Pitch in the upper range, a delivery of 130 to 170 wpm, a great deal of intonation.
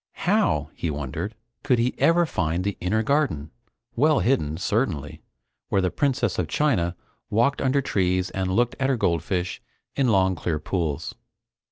No: very low, 95 Hz; average, 155 wpm; wide, 7.1 semitones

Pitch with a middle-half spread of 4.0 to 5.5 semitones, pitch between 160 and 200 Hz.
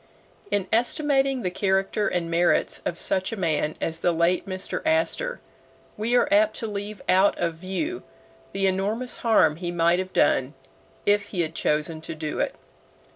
Yes: average, 4.3 semitones; high, 190 Hz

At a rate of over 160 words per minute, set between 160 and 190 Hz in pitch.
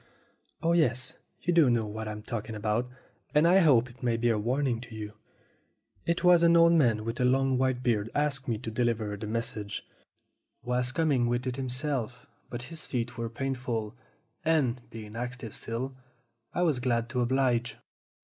No: average, 180 wpm; low, 125 Hz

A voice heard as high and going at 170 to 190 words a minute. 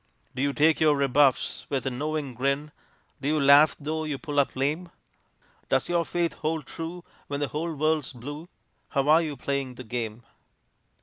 No: medium, 145 Hz; average, 180 wpm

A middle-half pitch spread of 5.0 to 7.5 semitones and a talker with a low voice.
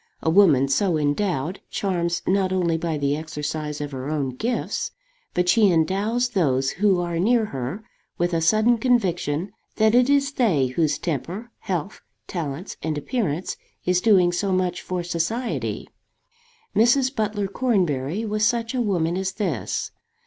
No: average, 5.3 semitones; medium, 180 Hz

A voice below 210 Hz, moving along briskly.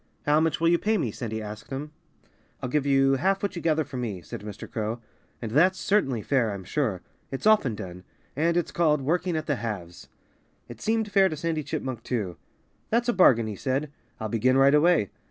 Yes: low, 135 Hz; fast, 210 wpm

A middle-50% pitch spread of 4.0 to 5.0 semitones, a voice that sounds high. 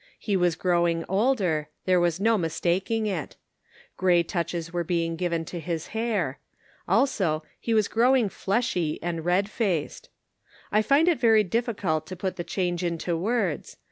No: average, 4.3 semitones; medium, 180 Hz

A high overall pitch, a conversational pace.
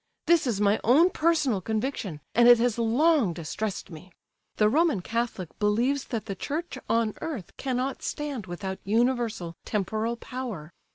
Yes: high, 230 Hz; average, 150 wpm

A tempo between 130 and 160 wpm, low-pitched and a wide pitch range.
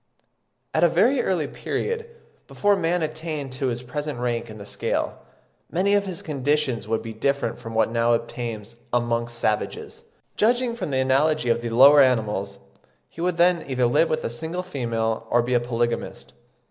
No: average, 175 wpm; low, 130 Hz; wide, 5.8 semitones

